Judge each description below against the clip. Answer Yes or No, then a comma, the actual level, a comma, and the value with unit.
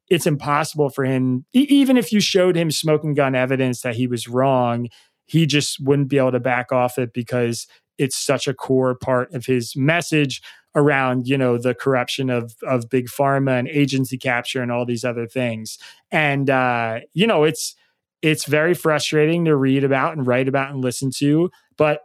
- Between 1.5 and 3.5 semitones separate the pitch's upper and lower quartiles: Yes, average, 3.1 semitones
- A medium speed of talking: Yes, average, 190 wpm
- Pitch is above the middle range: No, low, 135 Hz